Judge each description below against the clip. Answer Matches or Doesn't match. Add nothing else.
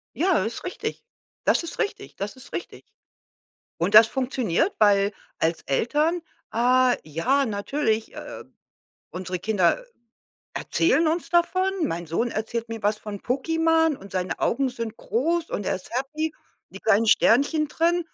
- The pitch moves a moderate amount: Doesn't match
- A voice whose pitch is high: Matches